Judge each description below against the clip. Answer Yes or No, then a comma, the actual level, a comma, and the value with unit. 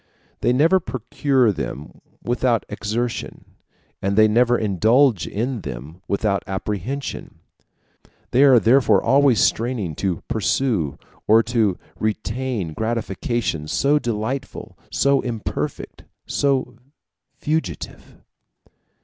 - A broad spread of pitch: No, average, 4.1 semitones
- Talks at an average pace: No, slow, 100 wpm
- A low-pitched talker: Yes, low, 115 Hz